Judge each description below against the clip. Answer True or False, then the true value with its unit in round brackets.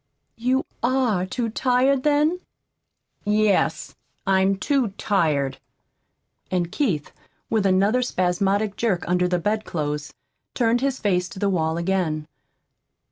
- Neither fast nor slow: False (115 wpm)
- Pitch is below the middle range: False (200 Hz)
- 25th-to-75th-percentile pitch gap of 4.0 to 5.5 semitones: True (5.2 semitones)